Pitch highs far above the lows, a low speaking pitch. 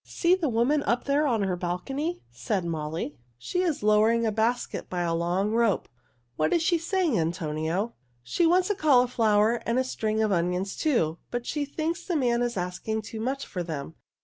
No: wide, 7.9 semitones; high, 225 Hz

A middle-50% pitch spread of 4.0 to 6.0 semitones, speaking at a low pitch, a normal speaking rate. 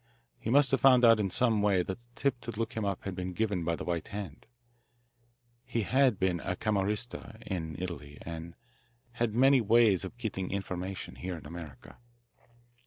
Yes: average, 4.6 semitones; low, 100 Hz; average, 180 wpm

